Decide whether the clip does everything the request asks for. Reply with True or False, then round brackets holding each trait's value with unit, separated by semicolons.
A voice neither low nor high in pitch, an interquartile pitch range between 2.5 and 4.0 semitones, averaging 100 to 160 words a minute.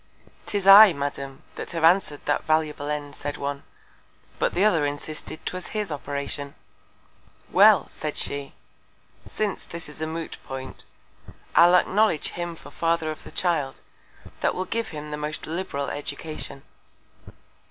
True (155 Hz; 3.4 semitones; 150 wpm)